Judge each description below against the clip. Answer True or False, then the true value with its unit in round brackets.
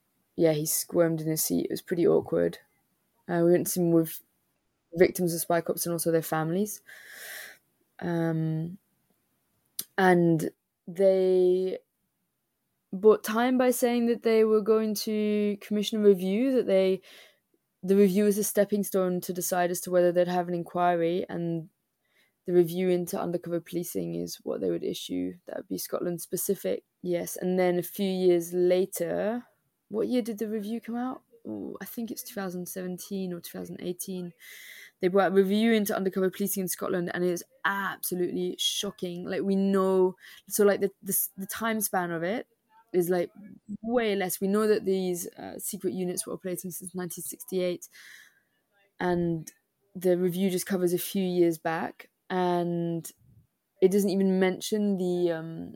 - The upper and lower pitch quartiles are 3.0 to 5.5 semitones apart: False (2.6 semitones)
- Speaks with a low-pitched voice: False (185 Hz)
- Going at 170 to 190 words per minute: False (160 wpm)